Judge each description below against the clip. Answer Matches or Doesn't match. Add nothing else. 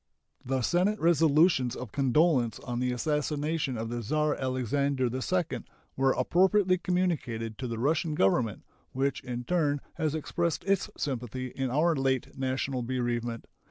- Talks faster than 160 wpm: Doesn't match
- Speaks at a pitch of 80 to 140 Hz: Matches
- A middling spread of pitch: Matches